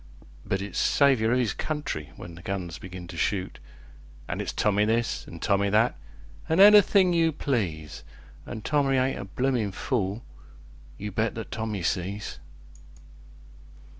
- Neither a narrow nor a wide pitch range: No, wide, 5.7 semitones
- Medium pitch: No, low, 105 Hz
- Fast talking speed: No, average, 145 wpm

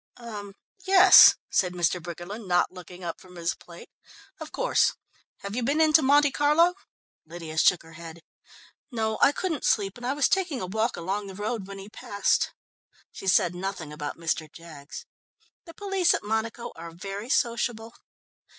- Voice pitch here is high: Yes, high, 200 Hz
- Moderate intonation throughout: No, wide, 6.2 semitones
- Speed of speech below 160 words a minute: No, average, 170 wpm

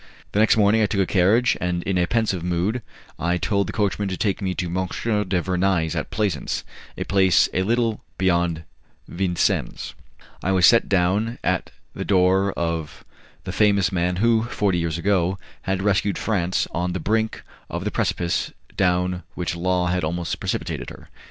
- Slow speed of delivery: No, average, 175 wpm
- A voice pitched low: Yes, very low, 95 Hz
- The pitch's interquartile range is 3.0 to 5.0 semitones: No, narrow, 2.6 semitones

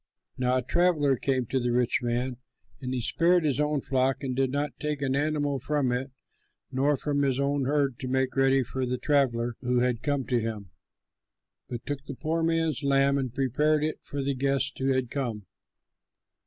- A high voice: No, low, 135 Hz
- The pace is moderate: Yes, average, 195 wpm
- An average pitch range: No, narrow, 2.3 semitones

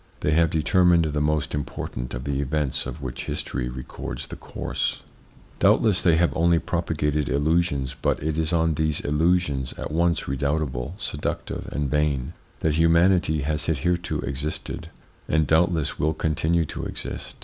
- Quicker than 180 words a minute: No, average, 150 wpm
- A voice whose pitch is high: No, very low, 75 Hz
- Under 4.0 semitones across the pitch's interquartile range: Yes, narrow, 2.6 semitones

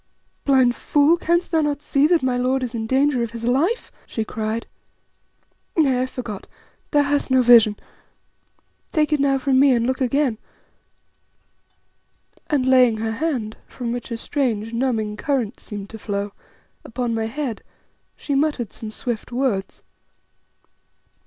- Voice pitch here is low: No, very high, 250 Hz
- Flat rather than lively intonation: No, average, 3.9 semitones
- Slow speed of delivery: No, average, 150 wpm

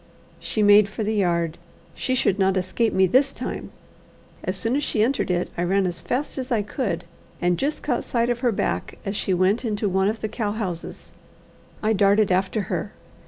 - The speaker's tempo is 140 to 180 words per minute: No, fast, 205 wpm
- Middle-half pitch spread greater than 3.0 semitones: Yes, average, 3.7 semitones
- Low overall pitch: No, high, 205 Hz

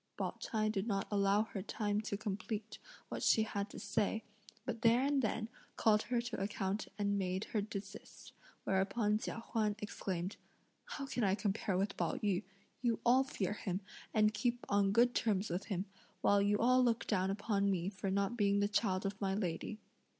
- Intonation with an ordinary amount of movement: No, narrow, 2.1 semitones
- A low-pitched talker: No, high, 205 Hz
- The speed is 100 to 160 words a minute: No, average, 185 wpm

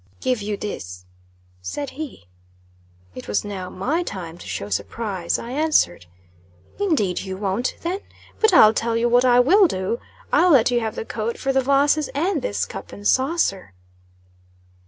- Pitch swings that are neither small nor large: No, wide, 7.0 semitones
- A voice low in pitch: No, high, 230 Hz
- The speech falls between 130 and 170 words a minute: Yes, average, 165 wpm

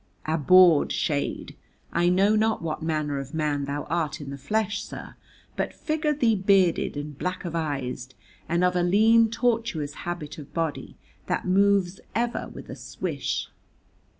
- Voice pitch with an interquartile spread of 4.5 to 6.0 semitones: Yes, average, 5.2 semitones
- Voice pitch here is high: No, medium, 175 Hz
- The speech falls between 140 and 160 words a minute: Yes, average, 150 wpm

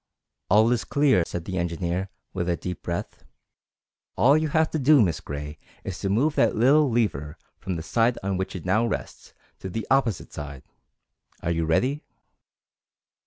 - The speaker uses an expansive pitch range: Yes, wide, 6.5 semitones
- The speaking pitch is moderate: No, very low, 95 Hz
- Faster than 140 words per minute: Yes, average, 175 wpm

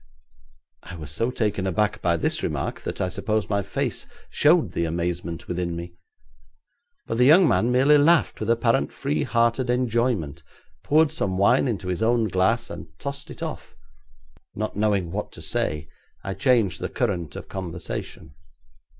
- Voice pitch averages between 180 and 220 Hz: No, low, 100 Hz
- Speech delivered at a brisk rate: No, average, 160 wpm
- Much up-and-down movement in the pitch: Yes, wide, 5.8 semitones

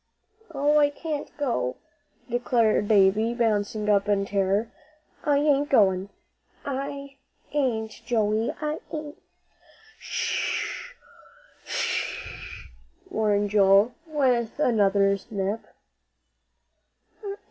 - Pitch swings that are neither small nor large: No, wide, 5.8 semitones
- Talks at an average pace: No, slow, 90 wpm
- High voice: Yes, high, 230 Hz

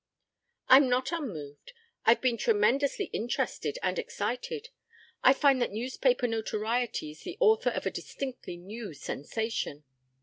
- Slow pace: Yes, slow, 130 wpm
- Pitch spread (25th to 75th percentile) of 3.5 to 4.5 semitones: Yes, average, 4.1 semitones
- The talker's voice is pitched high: Yes, high, 245 Hz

